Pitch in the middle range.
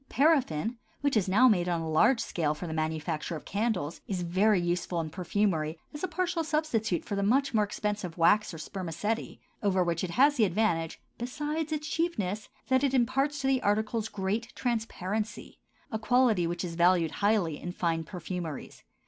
No: high, 205 Hz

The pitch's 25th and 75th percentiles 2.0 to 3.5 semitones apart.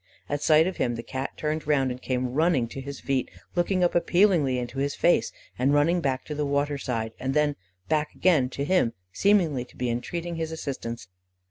No: average, 4.0 semitones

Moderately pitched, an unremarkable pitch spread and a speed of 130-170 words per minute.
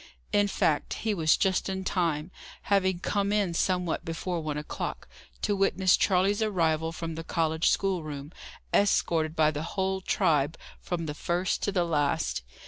Yes: medium, 170 Hz; average, 3.3 semitones; average, 155 wpm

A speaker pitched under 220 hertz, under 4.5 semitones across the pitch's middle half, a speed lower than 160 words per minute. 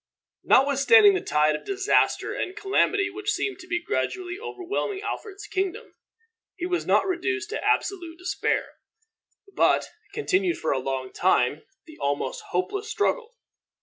No: very high, 375 Hz; average, 3.3 semitones; average, 140 wpm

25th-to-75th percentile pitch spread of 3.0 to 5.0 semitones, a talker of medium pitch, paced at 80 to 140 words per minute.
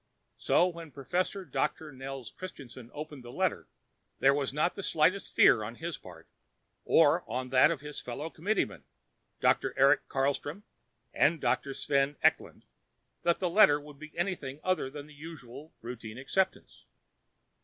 No: average, 4.1 semitones; medium, 145 Hz; average, 150 wpm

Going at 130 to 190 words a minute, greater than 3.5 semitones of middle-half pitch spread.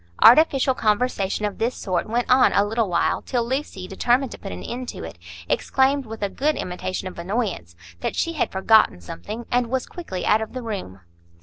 No: average, 200 wpm; average, 5.2 semitones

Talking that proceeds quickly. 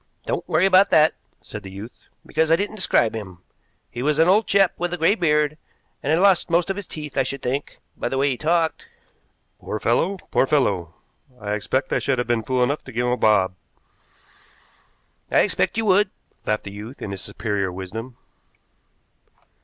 No: average, 195 wpm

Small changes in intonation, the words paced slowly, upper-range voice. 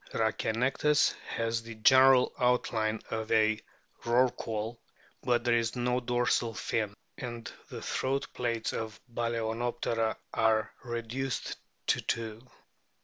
No: narrow, 1.8 semitones; slow, 110 wpm; low, 115 Hz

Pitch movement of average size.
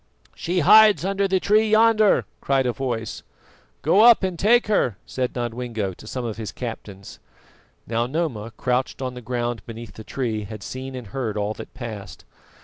No: wide, 8.0 semitones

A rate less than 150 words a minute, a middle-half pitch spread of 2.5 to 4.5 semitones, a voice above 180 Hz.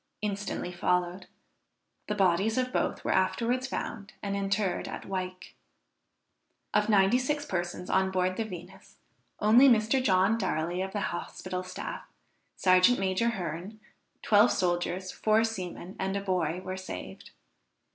Yes: slow, 135 wpm; average, 2.8 semitones; high, 190 Hz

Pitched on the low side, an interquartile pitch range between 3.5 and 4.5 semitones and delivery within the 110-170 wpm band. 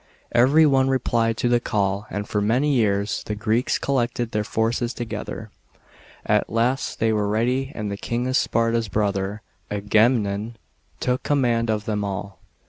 No: low, 115 Hz; average, 2.8 semitones; average, 165 wpm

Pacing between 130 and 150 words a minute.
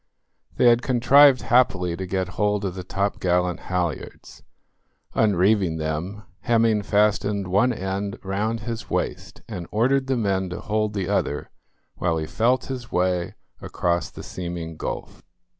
Yes: average, 140 wpm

